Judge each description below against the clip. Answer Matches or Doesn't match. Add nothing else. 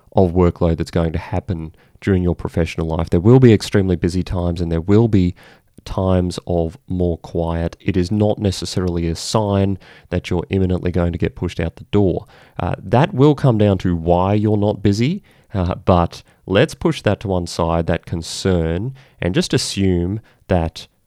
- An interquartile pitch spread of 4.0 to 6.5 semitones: Doesn't match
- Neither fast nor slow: Matches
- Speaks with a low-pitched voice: Matches